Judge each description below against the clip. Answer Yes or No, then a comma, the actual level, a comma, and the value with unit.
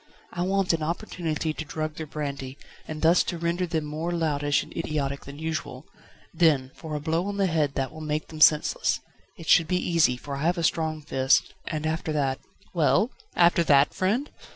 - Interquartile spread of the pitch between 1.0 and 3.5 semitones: Yes, narrow, 2.4 semitones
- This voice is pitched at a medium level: Yes, medium, 155 Hz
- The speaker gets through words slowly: No, average, 200 wpm